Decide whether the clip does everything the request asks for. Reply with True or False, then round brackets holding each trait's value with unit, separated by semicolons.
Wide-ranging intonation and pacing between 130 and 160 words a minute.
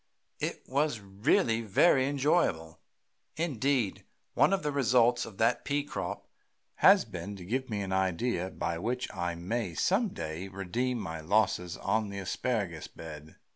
True (5.9 semitones; 150 wpm)